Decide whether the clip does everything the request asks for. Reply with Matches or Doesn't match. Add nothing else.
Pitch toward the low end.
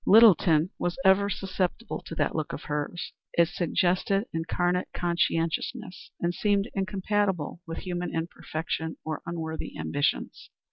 Doesn't match